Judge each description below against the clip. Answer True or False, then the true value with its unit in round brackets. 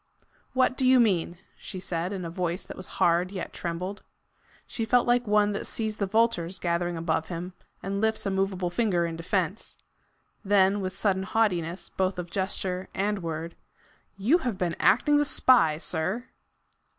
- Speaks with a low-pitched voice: False (190 Hz)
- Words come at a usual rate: True (170 wpm)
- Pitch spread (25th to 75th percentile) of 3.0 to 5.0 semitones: True (3.4 semitones)